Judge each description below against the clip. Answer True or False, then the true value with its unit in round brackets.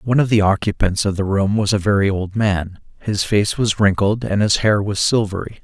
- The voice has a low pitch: True (100 Hz)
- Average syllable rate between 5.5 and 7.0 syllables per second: False (5.2 syllables/s)